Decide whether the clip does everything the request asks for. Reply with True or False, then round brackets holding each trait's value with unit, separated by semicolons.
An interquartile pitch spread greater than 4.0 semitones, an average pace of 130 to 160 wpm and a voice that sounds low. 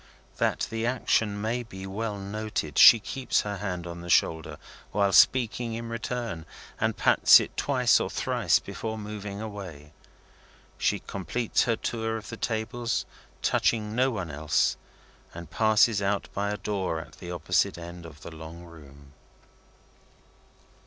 True (4.6 semitones; 150 wpm; 105 Hz)